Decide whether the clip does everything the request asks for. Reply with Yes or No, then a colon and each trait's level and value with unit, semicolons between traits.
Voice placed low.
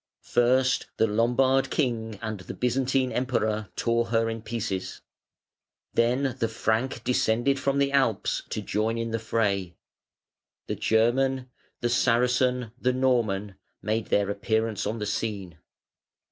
Yes: low, 115 Hz